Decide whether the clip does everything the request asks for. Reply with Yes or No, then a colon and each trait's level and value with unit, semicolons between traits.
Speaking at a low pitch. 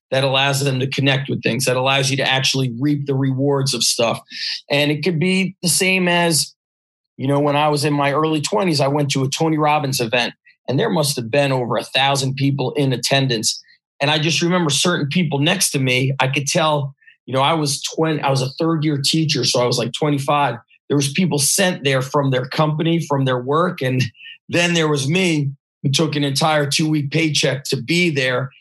No: medium, 145 Hz